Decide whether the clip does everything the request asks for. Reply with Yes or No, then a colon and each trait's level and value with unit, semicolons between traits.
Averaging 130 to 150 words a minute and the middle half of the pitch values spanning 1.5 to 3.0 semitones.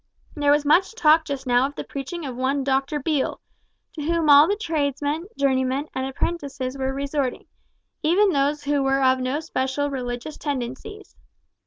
No: average, 165 wpm; narrow, 2.5 semitones